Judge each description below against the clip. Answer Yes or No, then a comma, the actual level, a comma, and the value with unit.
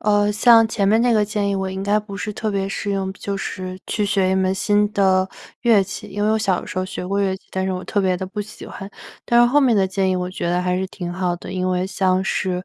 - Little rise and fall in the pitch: Yes, narrow, 1.8 semitones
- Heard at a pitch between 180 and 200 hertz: Yes, high, 195 Hz